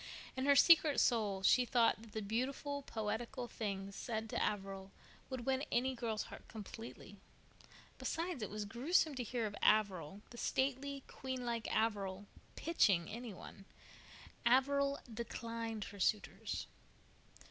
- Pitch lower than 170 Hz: No, high, 230 Hz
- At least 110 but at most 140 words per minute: Yes, slow, 135 wpm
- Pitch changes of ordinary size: Yes, average, 4.0 semitones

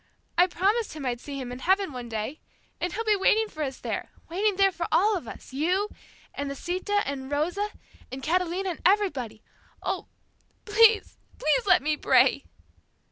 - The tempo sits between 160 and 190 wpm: Yes, average, 175 wpm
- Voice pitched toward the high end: Yes, very high, 355 Hz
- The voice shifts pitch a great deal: Yes, wide, 6.5 semitones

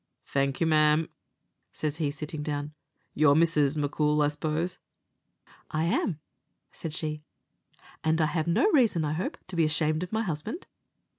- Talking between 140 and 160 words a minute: Yes, average, 155 wpm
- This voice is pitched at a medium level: Yes, medium, 155 Hz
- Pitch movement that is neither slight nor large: No, narrow, 1.8 semitones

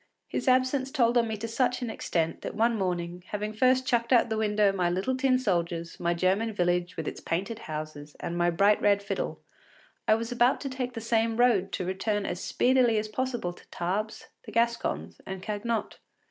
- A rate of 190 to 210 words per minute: Yes, average, 200 wpm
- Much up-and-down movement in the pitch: No, average, 4.9 semitones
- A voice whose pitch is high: Yes, high, 215 Hz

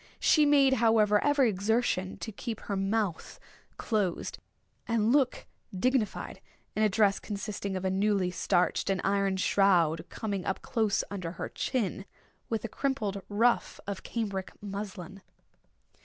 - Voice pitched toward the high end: Yes, high, 205 Hz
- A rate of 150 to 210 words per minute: No, average, 140 wpm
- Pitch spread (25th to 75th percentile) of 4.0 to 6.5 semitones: No, average, 2.9 semitones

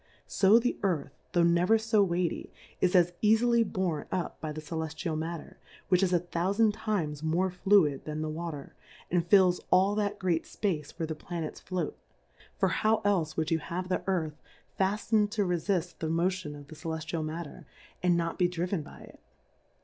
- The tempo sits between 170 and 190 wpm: Yes, average, 180 wpm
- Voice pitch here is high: No, medium, 175 Hz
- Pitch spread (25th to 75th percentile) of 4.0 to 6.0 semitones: No, average, 3.4 semitones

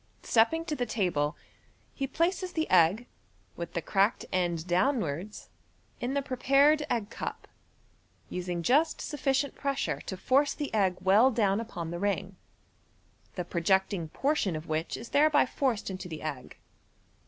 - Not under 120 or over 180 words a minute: Yes, average, 150 wpm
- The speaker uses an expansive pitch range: Yes, wide, 7.6 semitones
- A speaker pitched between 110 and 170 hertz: No, high, 205 Hz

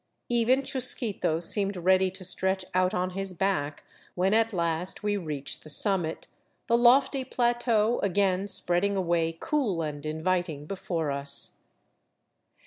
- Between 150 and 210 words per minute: No, slow, 135 wpm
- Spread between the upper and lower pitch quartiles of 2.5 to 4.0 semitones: No, average, 4.4 semitones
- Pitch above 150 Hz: Yes, high, 190 Hz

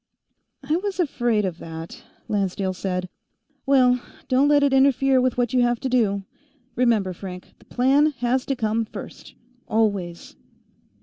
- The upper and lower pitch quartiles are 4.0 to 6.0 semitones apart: Yes, average, 5.2 semitones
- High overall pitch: Yes, high, 240 Hz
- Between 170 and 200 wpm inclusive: No, average, 145 wpm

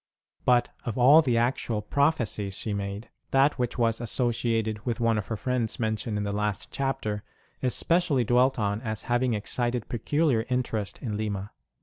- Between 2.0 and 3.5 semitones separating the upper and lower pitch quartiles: Yes, average, 3.0 semitones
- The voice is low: Yes, low, 115 Hz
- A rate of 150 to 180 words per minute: Yes, average, 165 wpm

